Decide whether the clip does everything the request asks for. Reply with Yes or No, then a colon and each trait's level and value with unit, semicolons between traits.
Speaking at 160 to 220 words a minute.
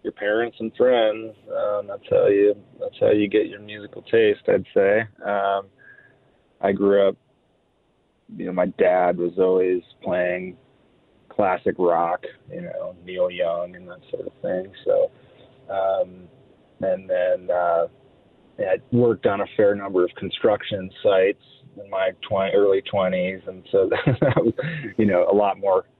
No: average, 145 wpm